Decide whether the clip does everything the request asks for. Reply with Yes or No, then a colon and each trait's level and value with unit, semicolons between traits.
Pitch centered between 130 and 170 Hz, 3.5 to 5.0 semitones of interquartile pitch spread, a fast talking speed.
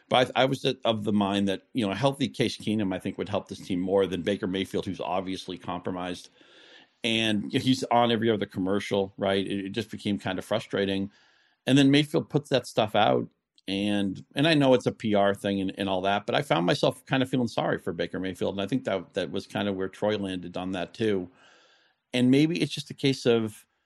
No: low, 105 Hz; average, 4.6 semitones; fast, 225 wpm